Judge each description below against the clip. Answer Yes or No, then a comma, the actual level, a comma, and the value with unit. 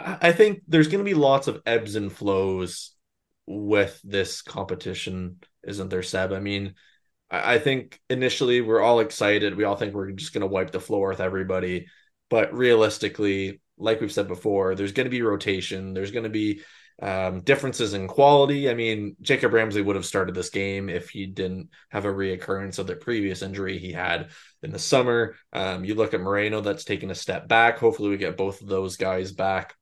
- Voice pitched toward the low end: Yes, low, 100 Hz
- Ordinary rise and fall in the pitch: Yes, average, 3.3 semitones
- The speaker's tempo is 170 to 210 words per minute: Yes, average, 195 wpm